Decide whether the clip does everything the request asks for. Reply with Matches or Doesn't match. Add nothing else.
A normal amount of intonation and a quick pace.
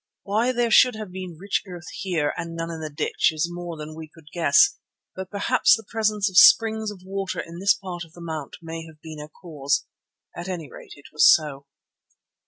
Matches